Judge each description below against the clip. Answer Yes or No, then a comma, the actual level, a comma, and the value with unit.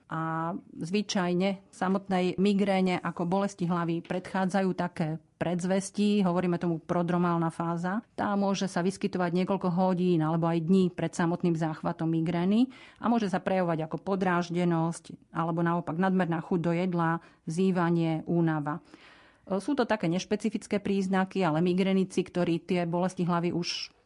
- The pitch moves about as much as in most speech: No, narrow, 2.3 semitones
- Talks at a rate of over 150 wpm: No, average, 135 wpm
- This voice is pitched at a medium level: Yes, medium, 180 Hz